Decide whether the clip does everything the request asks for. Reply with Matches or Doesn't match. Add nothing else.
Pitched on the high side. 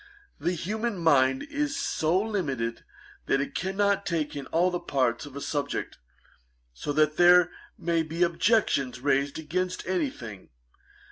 Doesn't match